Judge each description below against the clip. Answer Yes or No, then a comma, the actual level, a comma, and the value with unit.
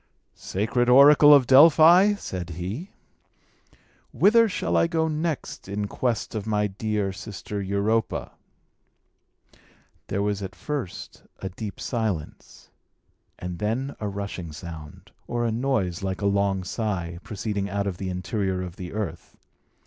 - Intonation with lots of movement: No, average, 4.6 semitones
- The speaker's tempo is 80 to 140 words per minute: Yes, slow, 135 wpm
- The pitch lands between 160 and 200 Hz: No, low, 105 Hz